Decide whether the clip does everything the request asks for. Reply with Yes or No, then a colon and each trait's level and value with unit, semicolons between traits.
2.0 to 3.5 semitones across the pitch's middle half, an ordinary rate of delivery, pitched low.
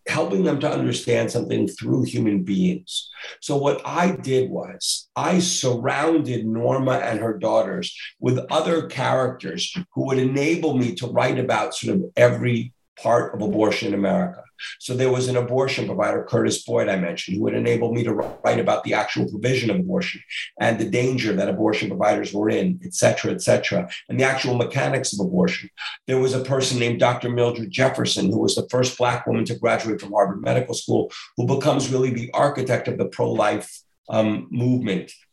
Yes: average, 2.8 semitones; average, 180 wpm; low, 125 Hz